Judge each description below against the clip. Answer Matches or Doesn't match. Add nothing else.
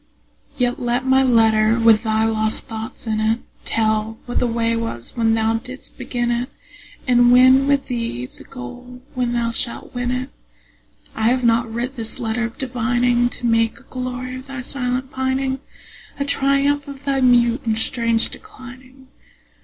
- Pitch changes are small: Matches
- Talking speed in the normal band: Matches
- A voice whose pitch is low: Doesn't match